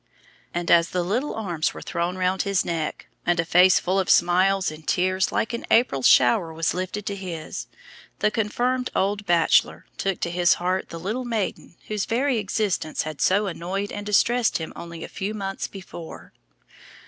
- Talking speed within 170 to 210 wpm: Yes, average, 180 wpm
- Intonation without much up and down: No, average, 3.3 semitones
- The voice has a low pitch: No, medium, 185 Hz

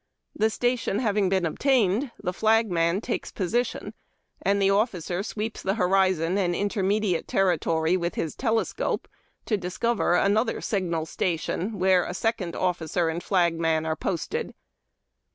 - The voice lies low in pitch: No, high, 190 Hz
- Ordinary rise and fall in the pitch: Yes, average, 3.8 semitones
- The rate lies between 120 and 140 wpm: Yes, slow, 135 wpm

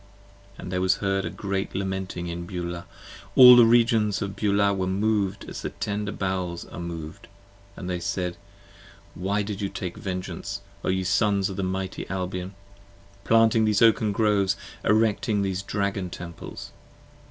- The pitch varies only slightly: Yes, narrow, 2.0 semitones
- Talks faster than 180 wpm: No, average, 165 wpm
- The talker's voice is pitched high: No, very low, 95 Hz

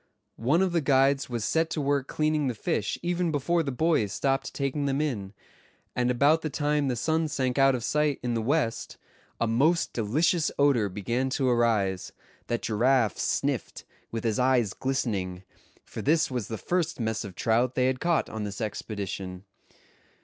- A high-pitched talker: No, low, 130 Hz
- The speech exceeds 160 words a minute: Yes, average, 180 wpm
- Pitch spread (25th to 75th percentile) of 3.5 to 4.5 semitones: No, average, 4.9 semitones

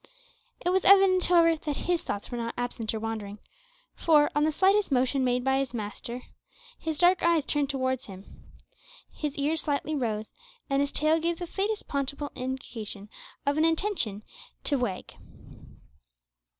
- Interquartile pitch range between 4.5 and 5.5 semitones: Yes, average, 5.1 semitones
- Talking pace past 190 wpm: No, average, 160 wpm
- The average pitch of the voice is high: Yes, very high, 280 Hz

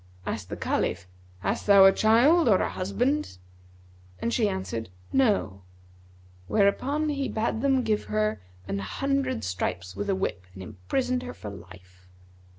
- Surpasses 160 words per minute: No, average, 150 wpm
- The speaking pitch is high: Yes, high, 200 Hz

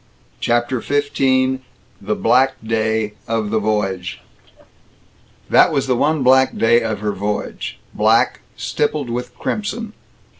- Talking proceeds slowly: Yes, slow, 120 wpm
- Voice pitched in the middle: No, low, 120 Hz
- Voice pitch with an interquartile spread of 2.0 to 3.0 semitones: No, average, 3.4 semitones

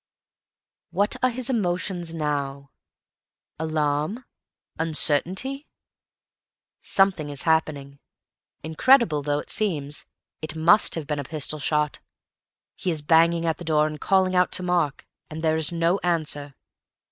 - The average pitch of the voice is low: No, medium, 160 Hz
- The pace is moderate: No, slow, 130 wpm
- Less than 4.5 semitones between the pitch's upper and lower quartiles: Yes, average, 3.4 semitones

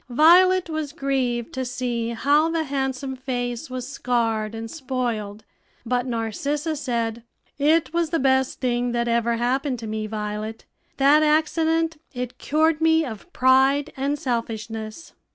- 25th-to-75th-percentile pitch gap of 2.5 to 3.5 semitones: No, average, 4.3 semitones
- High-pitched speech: Yes, very high, 260 Hz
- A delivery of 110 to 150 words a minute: Yes, average, 140 wpm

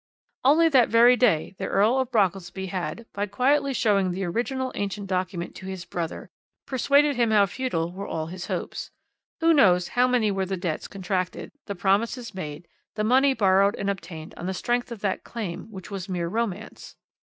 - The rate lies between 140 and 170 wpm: No, average, 185 wpm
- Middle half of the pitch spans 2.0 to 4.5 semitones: No, average, 4.9 semitones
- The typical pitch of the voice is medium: No, high, 200 Hz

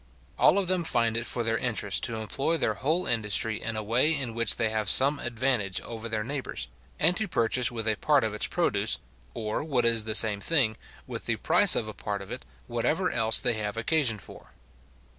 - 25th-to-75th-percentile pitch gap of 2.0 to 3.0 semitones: No, average, 3.7 semitones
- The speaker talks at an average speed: No, fast, 215 wpm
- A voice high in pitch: No, low, 115 Hz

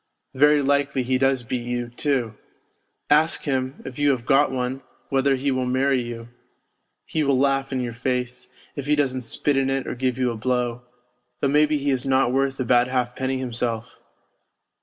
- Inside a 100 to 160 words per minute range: No, average, 185 wpm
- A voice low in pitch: Yes, low, 130 Hz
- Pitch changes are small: Yes, narrow, 1.8 semitones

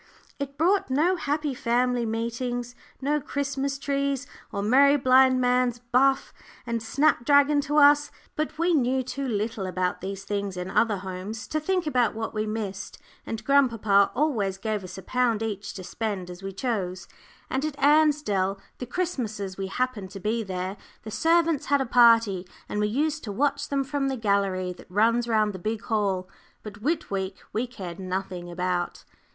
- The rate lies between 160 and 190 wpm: Yes, average, 175 wpm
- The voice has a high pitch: Yes, high, 230 Hz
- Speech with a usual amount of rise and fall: No, wide, 5.8 semitones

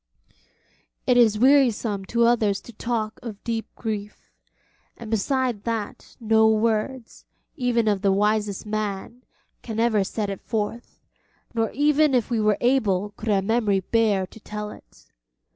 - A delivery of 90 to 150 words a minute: Yes, average, 145 wpm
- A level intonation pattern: Yes, narrow, 2.2 semitones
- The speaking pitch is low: No, high, 220 Hz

